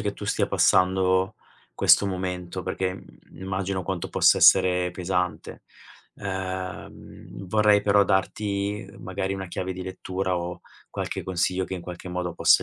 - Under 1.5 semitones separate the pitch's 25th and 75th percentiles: Yes, narrow, 1.1 semitones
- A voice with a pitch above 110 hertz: No, very low, 95 Hz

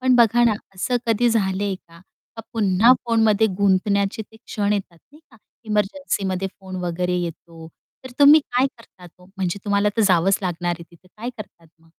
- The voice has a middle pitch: No, high, 200 Hz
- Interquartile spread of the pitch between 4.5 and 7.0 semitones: No, average, 3.7 semitones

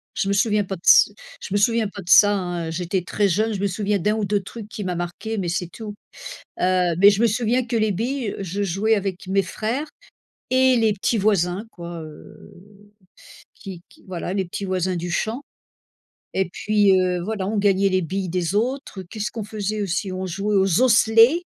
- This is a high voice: Yes, high, 200 Hz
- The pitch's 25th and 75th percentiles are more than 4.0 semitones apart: No, average, 2.8 semitones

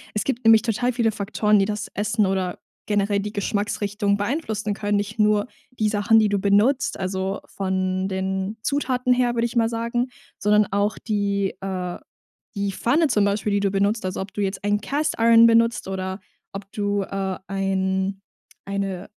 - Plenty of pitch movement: No, narrow, 2.4 semitones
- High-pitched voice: Yes, high, 205 Hz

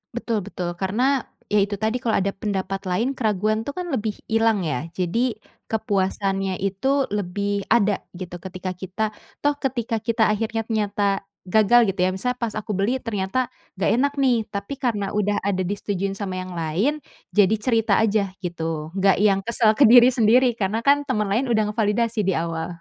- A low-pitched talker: No, high, 210 Hz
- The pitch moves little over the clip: No, average, 3.1 semitones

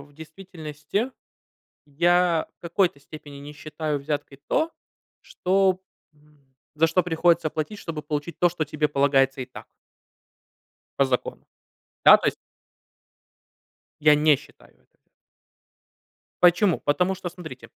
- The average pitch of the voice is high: No, medium, 155 Hz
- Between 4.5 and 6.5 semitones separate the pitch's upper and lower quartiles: No, average, 3.3 semitones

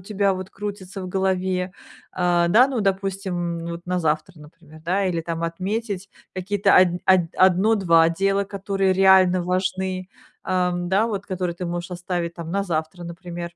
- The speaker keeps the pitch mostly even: Yes, narrow, 2.1 semitones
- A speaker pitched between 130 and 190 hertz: Yes, medium, 185 Hz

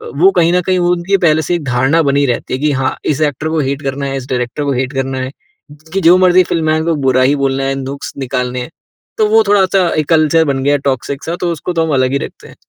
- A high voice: No, medium, 145 Hz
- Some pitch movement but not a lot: Yes, average, 4.0 semitones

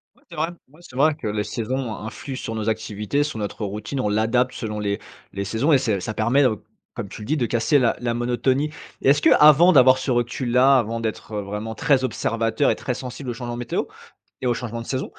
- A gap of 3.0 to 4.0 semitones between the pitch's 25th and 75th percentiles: Yes, average, 3.4 semitones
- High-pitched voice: No, low, 120 Hz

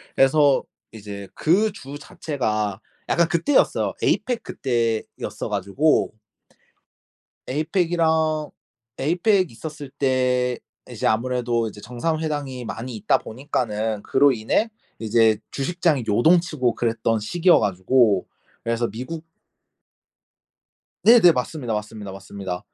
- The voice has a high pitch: No, low, 130 Hz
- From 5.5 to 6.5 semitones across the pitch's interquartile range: Yes, wide, 6.1 semitones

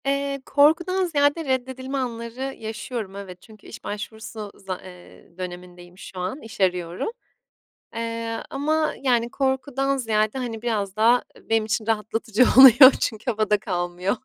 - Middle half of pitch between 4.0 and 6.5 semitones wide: Yes, average, 4.7 semitones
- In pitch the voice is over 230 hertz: No, high, 225 Hz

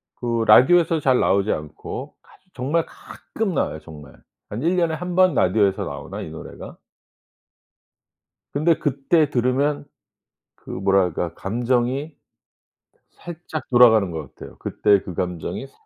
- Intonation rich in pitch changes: Yes, wide, 8.3 semitones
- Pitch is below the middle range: Yes, low, 125 Hz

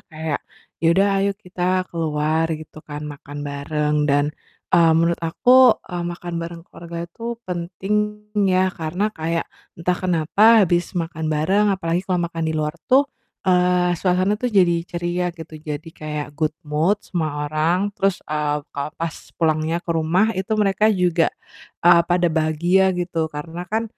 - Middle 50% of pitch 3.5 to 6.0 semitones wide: No, average, 2.9 semitones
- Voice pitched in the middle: Yes, medium, 170 Hz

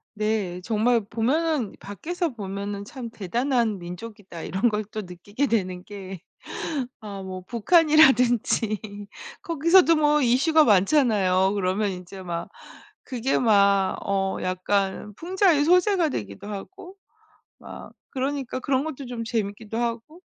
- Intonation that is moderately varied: No, wide, 6.1 semitones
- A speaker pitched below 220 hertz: No, high, 225 Hz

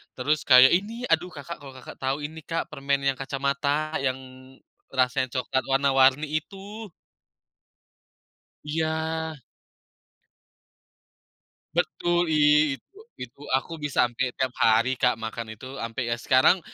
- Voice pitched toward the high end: No, low, 135 Hz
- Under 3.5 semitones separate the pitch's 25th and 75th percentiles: Yes, average, 3.1 semitones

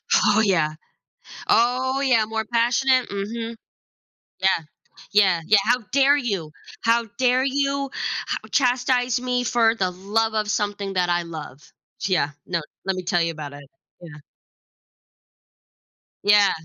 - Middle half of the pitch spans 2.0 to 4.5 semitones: No, average, 5.2 semitones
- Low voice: No, high, 215 Hz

